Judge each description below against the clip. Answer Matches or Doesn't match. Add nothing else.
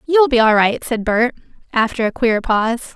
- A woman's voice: Matches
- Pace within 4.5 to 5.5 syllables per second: Matches